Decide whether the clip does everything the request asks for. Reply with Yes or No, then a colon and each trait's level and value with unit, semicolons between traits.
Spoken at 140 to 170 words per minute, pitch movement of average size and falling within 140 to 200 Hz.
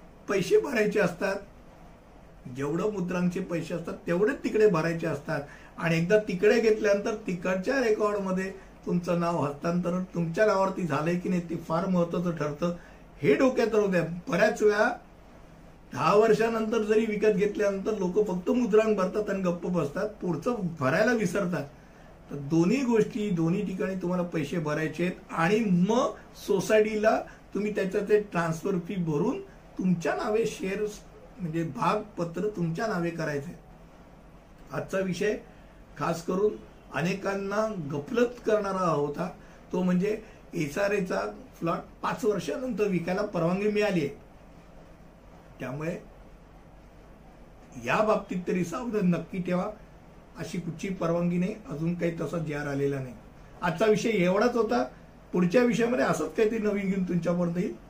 No: average, 130 wpm; average, 3.9 semitones; high, 190 Hz